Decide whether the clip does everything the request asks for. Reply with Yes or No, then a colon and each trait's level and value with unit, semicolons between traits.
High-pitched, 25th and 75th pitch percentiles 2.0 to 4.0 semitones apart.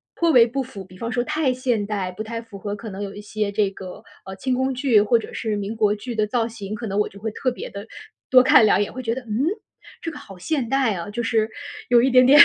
Yes: high, 225 Hz; average, 3.7 semitones